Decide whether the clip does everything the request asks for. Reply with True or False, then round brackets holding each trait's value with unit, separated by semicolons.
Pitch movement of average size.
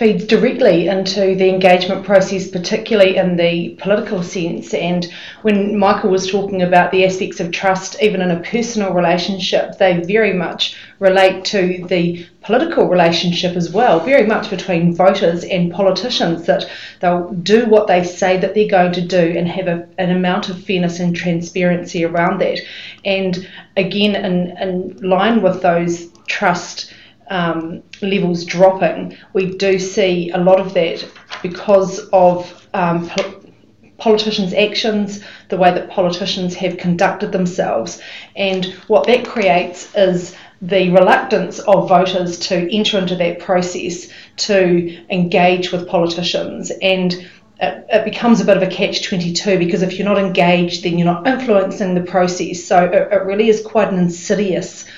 False (1.8 semitones)